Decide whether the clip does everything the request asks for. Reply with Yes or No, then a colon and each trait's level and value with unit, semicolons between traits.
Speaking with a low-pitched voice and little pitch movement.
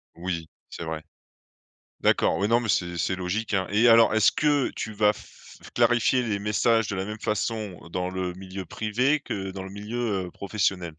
No: low, 100 Hz; average, 3.4 semitones